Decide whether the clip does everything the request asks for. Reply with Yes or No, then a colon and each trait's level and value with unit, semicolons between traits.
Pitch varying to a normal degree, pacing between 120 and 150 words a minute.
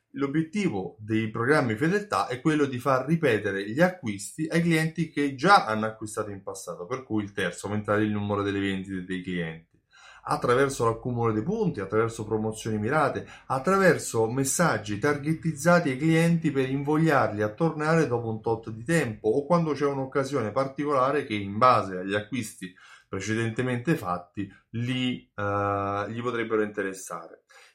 No: wide, 5.9 semitones; average, 145 wpm